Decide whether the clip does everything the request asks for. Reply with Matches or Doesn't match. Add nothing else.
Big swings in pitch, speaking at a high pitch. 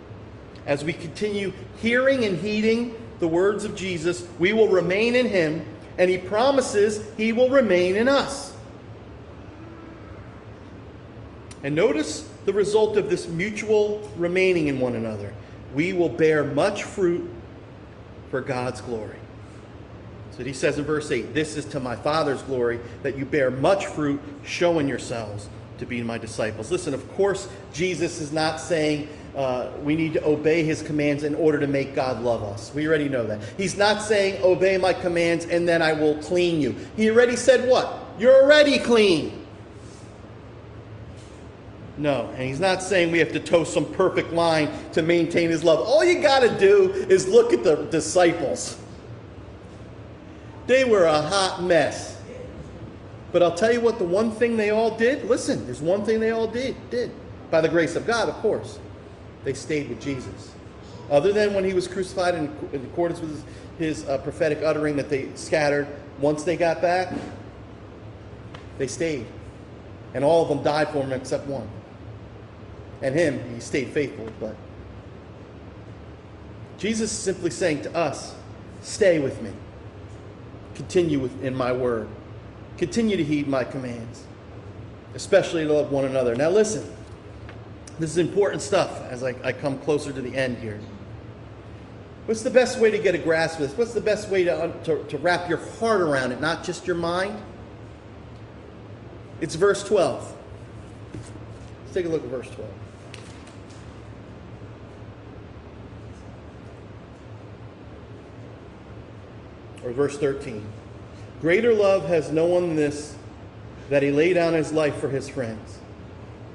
Doesn't match